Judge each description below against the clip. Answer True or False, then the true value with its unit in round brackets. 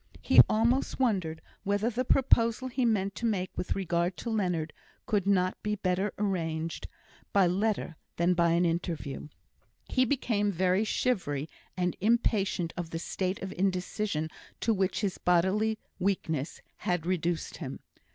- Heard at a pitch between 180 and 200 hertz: True (190 Hz)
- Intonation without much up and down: False (3.7 semitones)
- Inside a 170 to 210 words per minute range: False (145 wpm)